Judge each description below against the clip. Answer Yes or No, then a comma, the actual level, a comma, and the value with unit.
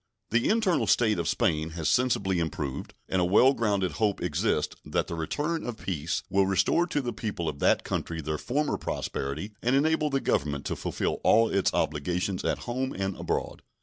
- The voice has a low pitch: Yes, low, 100 Hz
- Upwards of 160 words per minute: Yes, average, 185 wpm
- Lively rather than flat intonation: Yes, wide, 7.4 semitones